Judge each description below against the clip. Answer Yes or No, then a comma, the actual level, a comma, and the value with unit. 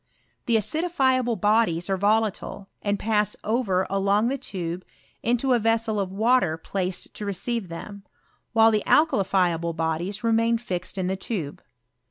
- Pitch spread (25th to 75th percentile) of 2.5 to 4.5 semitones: Yes, average, 3.6 semitones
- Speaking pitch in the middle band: No, high, 205 Hz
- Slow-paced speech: No, average, 155 wpm